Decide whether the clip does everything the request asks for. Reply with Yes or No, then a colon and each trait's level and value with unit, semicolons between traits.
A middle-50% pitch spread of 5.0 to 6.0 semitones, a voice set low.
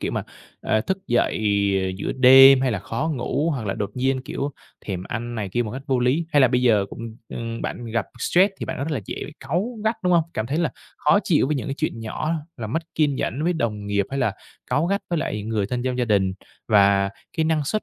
Yes: wide, 5.6 semitones; low, 130 Hz